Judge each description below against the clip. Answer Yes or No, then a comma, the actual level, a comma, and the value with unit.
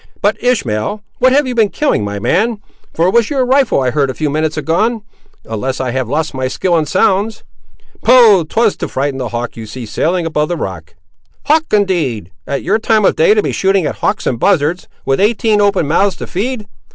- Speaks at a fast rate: Yes, fast, 210 wpm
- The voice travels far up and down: Yes, wide, 8.7 semitones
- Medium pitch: Yes, medium, 175 Hz